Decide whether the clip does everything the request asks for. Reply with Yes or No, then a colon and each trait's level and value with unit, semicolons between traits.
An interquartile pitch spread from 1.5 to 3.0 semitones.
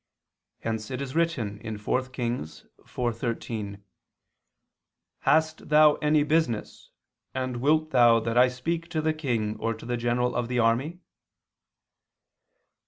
No: average, 4.7 semitones